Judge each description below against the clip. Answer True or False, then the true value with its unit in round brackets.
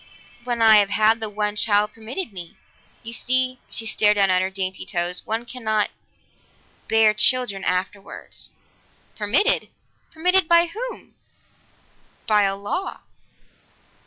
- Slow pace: True (130 wpm)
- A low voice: False (215 Hz)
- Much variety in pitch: False (3.8 semitones)